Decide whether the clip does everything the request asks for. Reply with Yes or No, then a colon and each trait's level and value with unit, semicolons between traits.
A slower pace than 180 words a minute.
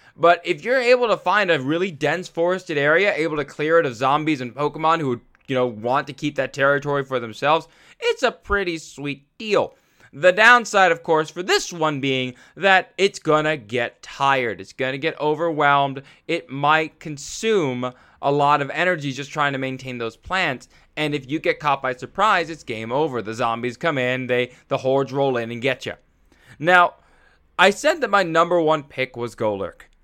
No: average, 200 wpm